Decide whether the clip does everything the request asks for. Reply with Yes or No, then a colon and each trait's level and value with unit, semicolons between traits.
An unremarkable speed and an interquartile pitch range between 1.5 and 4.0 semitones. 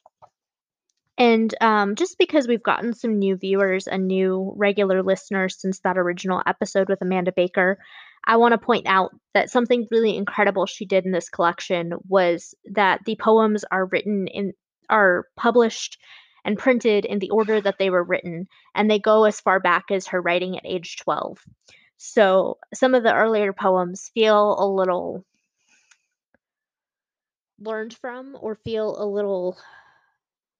Yes: average, 155 wpm; average, 2.8 semitones